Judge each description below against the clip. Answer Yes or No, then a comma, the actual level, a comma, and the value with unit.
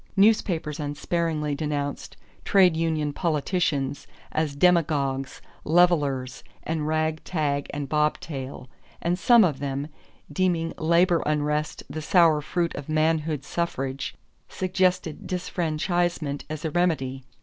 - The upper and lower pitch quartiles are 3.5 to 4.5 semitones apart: No, average, 3.1 semitones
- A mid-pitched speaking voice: Yes, medium, 155 Hz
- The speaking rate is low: Yes, slow, 110 wpm